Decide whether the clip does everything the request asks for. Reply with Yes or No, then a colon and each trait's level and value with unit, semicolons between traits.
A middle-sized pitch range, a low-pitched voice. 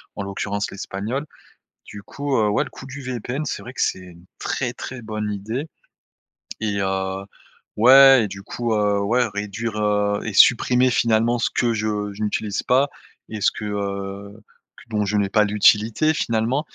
Yes: average, 3.1 semitones; low, 105 Hz